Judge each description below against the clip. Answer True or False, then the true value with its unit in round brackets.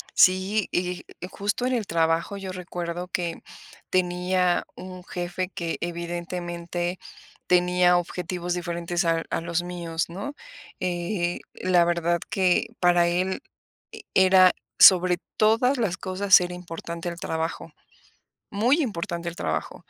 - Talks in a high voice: False (180 Hz)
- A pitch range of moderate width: False (1.4 semitones)